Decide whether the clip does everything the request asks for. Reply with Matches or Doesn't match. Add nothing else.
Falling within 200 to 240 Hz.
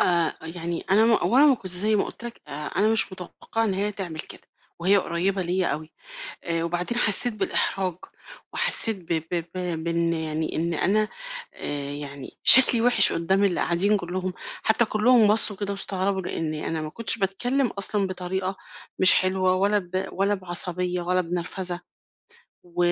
Doesn't match